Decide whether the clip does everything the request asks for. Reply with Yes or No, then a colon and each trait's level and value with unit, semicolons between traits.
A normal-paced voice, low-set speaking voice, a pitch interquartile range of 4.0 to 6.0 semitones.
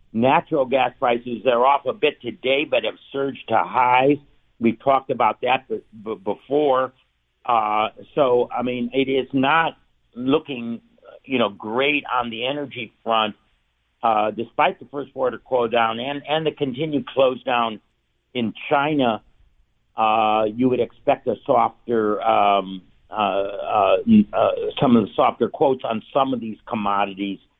Yes: average, 150 wpm; low, 120 Hz; average, 4.3 semitones